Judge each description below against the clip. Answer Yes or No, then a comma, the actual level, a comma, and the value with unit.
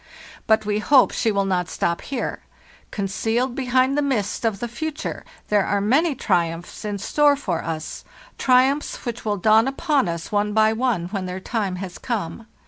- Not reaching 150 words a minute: No, average, 170 wpm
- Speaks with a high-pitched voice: Yes, high, 220 Hz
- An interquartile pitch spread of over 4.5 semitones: Yes, average, 5.0 semitones